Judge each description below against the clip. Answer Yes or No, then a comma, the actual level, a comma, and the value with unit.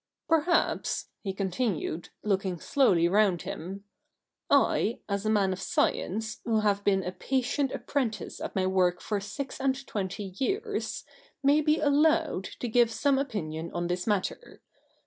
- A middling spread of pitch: No, wide, 6.2 semitones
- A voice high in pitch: Yes, high, 210 Hz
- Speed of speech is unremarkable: Yes, average, 155 wpm